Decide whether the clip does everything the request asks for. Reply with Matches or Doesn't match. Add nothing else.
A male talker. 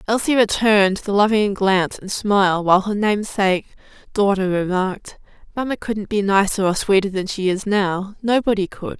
Doesn't match